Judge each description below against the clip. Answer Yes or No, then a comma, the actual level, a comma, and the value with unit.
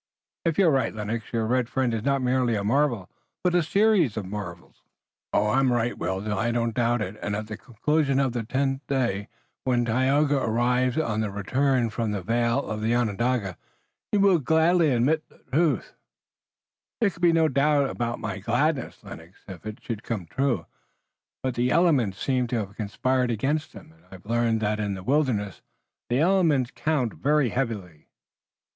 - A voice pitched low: Yes, low, 120 Hz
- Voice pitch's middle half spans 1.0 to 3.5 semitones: No, average, 4.6 semitones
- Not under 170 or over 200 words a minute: Yes, average, 175 wpm